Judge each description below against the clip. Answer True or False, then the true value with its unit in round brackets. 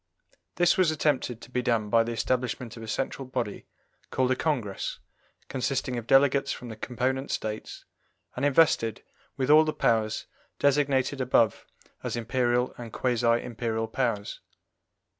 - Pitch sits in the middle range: False (125 Hz)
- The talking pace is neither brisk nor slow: True (145 wpm)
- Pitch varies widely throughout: False (2.8 semitones)